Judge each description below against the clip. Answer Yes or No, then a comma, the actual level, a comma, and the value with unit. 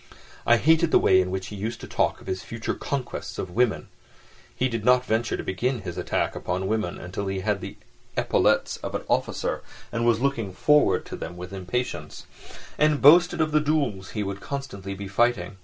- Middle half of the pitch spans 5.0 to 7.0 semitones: Yes, wide, 5.4 semitones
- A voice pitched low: Yes, low, 110 Hz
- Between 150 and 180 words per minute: No, average, 200 wpm